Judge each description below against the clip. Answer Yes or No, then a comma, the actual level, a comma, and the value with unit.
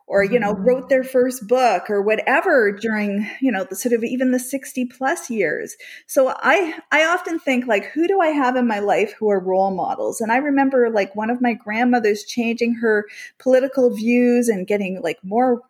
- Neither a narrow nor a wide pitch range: Yes, average, 3.7 semitones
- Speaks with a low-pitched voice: No, high, 245 Hz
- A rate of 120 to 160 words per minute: No, fast, 205 wpm